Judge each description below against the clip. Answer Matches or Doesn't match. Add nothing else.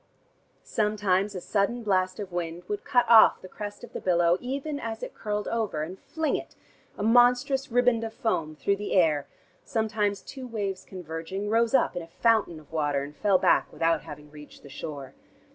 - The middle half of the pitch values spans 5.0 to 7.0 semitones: Matches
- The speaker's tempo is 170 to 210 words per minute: Matches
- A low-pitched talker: Doesn't match